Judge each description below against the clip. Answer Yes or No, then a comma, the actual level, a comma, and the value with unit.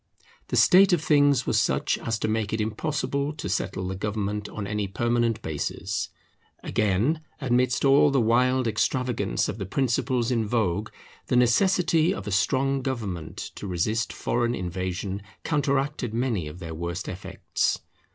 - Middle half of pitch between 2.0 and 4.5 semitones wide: No, average, 5.1 semitones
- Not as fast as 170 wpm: Yes, average, 150 wpm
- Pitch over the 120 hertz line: No, low, 115 Hz